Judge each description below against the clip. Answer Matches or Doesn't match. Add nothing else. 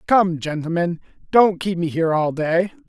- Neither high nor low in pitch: Matches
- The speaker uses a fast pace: Doesn't match